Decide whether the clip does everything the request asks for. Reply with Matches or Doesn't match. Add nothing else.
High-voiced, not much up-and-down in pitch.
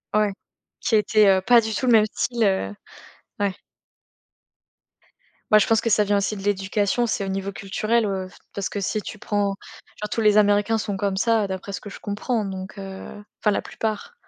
Matches